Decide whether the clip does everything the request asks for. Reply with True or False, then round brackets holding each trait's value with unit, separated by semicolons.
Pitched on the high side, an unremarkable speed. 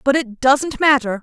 True (265 Hz; 195 wpm)